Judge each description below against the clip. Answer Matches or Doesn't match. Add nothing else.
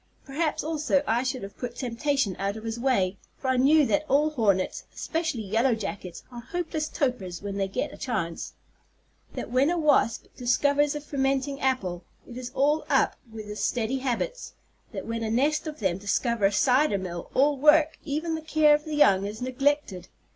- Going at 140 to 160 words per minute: Doesn't match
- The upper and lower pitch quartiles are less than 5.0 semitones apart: Doesn't match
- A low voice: Doesn't match